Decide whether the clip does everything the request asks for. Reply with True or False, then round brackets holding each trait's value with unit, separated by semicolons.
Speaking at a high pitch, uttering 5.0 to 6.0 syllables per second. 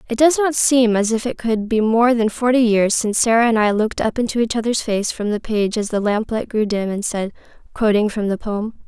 True (220 Hz; 5.5 syllables/s)